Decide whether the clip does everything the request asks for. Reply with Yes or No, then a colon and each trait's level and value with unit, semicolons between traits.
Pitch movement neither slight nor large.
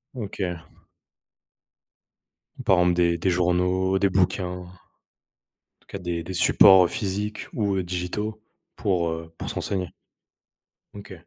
No: narrow, 2.0 semitones